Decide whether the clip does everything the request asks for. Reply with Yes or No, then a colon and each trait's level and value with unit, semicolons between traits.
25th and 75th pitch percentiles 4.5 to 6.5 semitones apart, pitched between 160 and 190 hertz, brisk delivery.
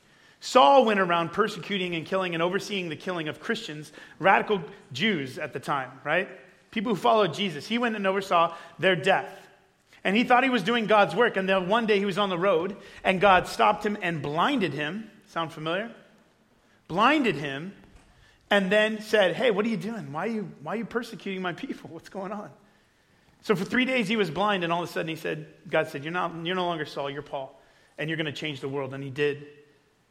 Yes: average, 5.3 semitones; medium, 185 Hz; fast, 220 wpm